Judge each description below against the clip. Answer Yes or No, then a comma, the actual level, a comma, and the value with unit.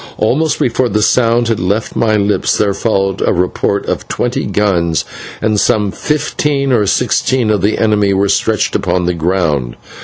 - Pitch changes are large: No, average, 3.2 semitones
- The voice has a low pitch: Yes, low, 105 Hz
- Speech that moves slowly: No, average, 165 wpm